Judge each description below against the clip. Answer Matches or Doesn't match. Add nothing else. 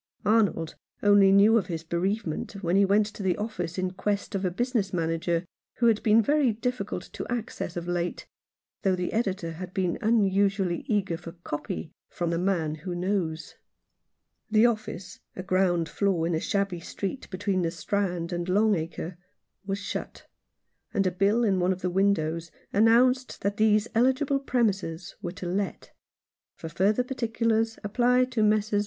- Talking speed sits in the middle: Matches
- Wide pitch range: Doesn't match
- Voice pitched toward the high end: Matches